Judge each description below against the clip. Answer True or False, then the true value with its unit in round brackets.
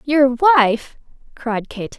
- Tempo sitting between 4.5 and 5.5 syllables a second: False (4.0 syllables/s)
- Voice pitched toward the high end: True (260 Hz)